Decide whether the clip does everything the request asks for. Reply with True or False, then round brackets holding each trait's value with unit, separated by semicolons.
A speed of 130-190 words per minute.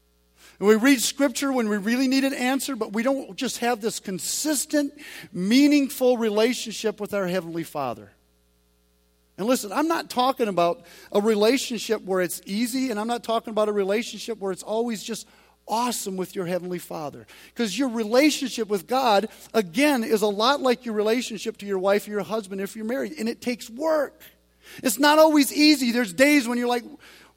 True (185 wpm)